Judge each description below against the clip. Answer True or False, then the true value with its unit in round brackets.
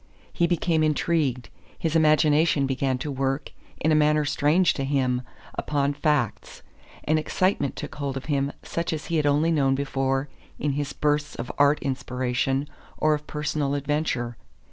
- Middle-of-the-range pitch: True (145 Hz)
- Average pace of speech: True (160 wpm)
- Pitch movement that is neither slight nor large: False (2.3 semitones)